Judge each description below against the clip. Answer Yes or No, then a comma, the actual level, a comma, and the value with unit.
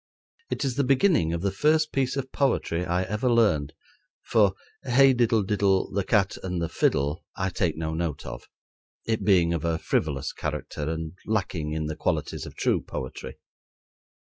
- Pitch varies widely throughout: Yes, wide, 6.5 semitones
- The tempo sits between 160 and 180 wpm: Yes, average, 170 wpm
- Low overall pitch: Yes, very low, 95 Hz